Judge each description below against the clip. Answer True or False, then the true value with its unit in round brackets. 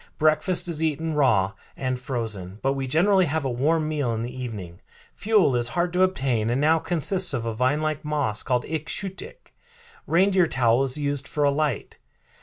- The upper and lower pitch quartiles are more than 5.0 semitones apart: False (4.7 semitones)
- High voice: False (145 Hz)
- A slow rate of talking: False (195 wpm)